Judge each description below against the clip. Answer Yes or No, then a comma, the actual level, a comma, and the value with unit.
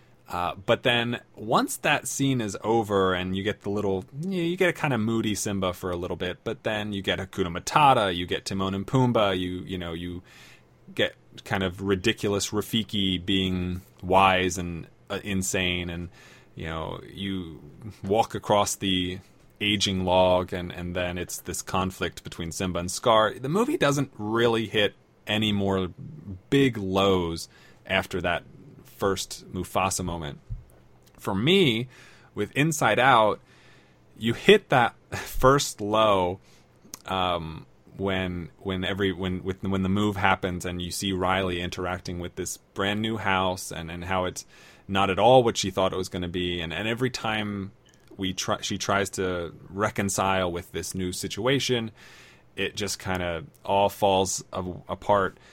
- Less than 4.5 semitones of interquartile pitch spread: Yes, average, 2.9 semitones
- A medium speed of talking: Yes, average, 165 wpm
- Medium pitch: No, very low, 95 Hz